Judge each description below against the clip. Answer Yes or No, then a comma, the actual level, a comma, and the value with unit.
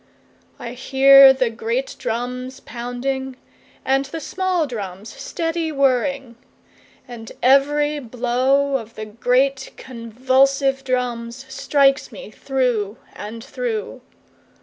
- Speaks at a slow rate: Yes, slow, 90 wpm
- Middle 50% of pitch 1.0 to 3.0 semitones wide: Yes, narrow, 2.4 semitones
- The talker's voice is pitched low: No, very high, 260 Hz